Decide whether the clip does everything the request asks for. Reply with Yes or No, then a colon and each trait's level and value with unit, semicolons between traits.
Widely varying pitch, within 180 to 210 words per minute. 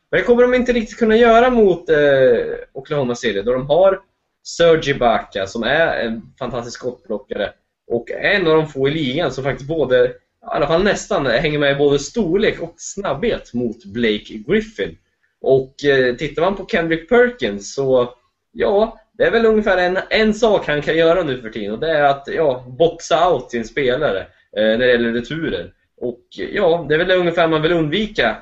Yes: wide, 8.3 semitones; average, 190 wpm